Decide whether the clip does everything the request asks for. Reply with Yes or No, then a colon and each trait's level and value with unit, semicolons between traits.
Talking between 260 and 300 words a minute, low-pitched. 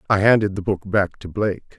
No: fast, 235 wpm; low, 100 Hz